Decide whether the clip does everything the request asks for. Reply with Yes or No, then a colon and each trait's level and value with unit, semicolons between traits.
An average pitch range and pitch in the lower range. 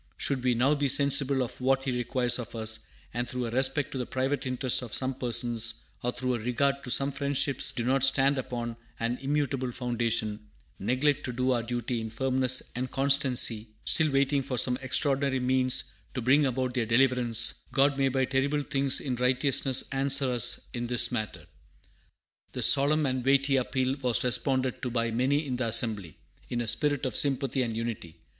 No: narrow, 2.1 semitones; low, 130 Hz